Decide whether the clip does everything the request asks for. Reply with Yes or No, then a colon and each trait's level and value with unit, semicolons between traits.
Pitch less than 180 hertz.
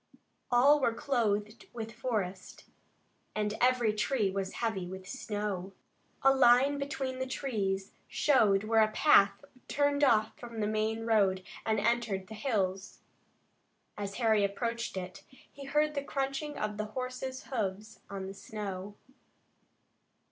No: high, 220 Hz